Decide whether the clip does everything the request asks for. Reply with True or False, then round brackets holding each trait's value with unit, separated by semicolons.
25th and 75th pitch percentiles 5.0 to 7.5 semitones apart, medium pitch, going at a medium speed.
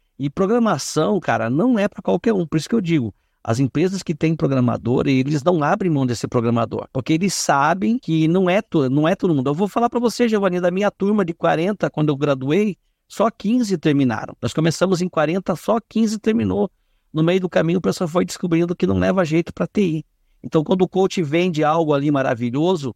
False (5.3 semitones; 170 Hz; 210 wpm)